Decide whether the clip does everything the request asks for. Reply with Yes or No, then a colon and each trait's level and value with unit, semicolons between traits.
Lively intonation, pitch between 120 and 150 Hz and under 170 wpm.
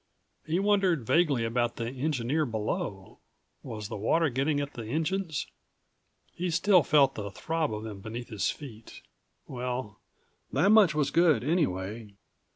Yes: wide, 6.4 semitones; low, 135 Hz; average, 145 wpm